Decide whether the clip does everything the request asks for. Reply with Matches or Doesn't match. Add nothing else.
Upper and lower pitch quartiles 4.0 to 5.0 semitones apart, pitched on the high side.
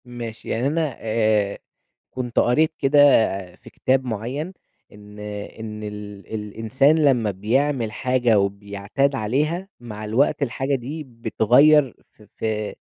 Doesn't match